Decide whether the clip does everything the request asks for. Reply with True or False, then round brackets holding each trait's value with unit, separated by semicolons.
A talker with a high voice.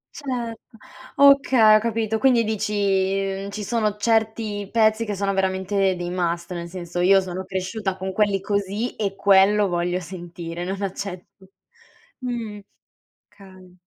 True (195 Hz)